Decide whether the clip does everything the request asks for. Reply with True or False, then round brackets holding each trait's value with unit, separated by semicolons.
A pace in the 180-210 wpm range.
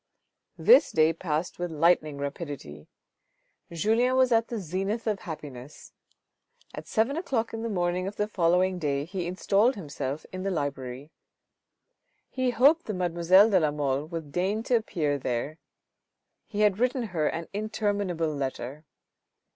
False (145 wpm)